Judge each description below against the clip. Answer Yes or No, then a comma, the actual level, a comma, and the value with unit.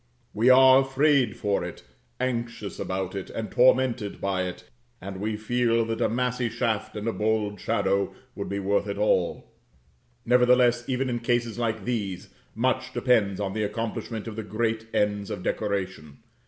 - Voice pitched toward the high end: No, low, 110 Hz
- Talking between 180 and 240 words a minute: No, average, 165 wpm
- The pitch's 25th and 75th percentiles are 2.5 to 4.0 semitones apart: Yes, average, 3.3 semitones